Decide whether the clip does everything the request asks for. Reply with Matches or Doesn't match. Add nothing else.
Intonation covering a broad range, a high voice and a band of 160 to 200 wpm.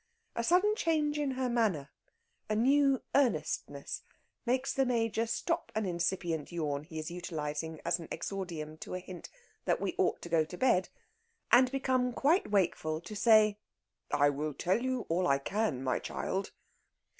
Matches